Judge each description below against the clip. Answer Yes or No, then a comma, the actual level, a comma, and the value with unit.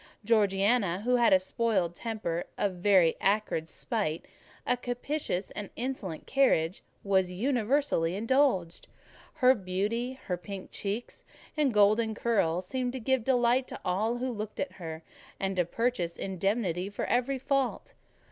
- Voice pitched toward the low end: No, high, 210 Hz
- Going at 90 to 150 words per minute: Yes, average, 140 wpm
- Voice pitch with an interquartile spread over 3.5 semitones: Yes, average, 5.0 semitones